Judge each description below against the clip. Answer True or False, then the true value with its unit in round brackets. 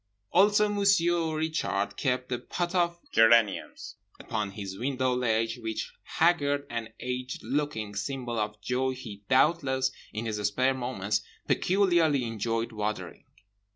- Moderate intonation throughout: False (5.7 semitones)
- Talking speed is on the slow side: True (125 wpm)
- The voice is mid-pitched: False (125 Hz)